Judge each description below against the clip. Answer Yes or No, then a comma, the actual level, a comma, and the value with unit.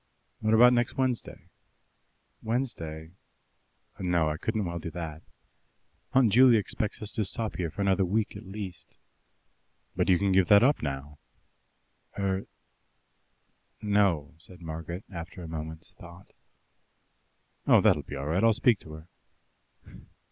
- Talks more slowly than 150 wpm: Yes, slow, 135 wpm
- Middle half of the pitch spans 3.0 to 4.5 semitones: No, average, 5.1 semitones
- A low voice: Yes, very low, 95 Hz